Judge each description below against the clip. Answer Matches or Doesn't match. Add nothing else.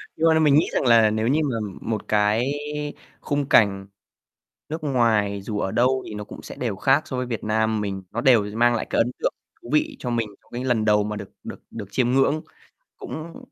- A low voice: Matches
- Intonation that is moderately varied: Matches